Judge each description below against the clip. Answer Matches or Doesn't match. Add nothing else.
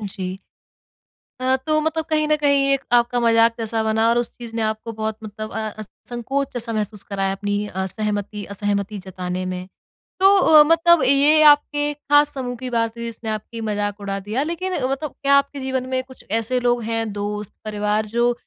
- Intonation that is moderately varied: Matches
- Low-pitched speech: Doesn't match